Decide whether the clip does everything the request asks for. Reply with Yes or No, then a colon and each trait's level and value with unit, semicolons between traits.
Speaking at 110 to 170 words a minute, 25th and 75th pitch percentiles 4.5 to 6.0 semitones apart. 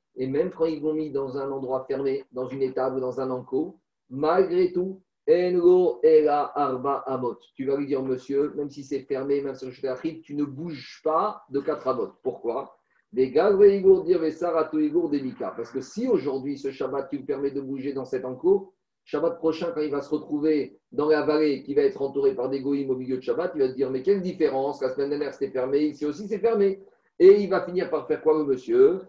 No: fast, 220 wpm; average, 5.1 semitones